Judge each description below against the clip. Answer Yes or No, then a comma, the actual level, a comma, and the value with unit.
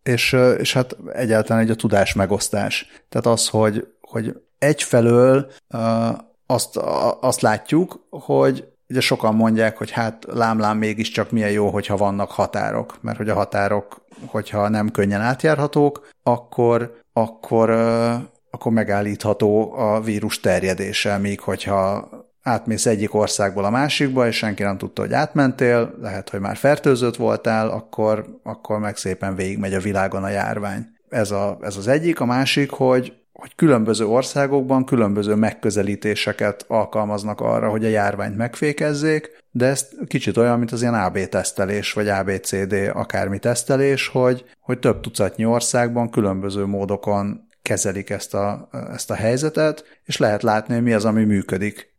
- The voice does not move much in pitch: No, average, 3.1 semitones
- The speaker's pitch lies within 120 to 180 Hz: No, low, 110 Hz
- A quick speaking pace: No, average, 145 wpm